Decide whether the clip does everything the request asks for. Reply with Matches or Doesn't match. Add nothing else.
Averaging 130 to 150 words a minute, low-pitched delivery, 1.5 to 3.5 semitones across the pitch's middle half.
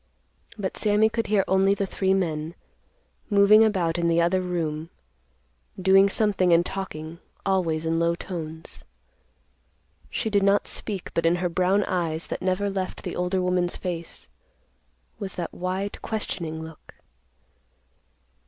Doesn't match